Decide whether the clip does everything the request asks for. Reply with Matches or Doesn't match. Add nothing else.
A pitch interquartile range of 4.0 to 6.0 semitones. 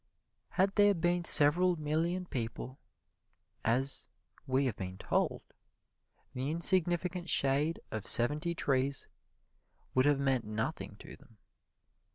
Matches